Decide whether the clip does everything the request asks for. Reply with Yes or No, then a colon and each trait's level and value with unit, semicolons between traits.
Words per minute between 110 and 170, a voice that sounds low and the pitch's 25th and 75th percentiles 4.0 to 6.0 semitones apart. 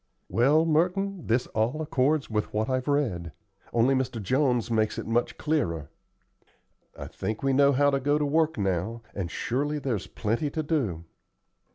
Yes: average, 165 wpm; low, 130 Hz; average, 5.1 semitones